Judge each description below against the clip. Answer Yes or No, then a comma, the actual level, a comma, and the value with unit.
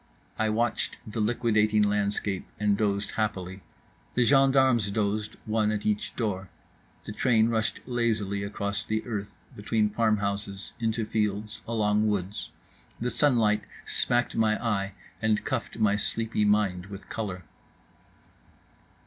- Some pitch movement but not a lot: No, narrow, 1.8 semitones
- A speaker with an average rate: No, slow, 125 wpm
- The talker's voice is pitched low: Yes, low, 105 Hz